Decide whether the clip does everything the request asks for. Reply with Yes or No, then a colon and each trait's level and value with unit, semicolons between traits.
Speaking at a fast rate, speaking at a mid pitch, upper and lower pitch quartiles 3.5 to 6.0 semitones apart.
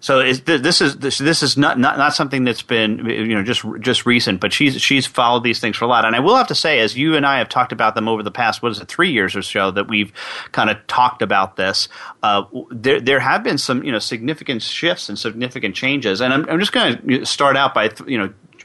No: fast, 265 wpm; low, 125 Hz; average, 3.8 semitones